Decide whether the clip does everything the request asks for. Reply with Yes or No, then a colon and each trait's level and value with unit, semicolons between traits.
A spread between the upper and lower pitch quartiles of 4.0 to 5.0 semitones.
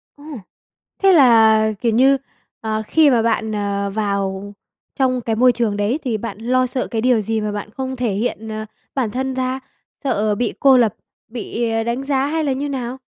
No: average, 3.3 semitones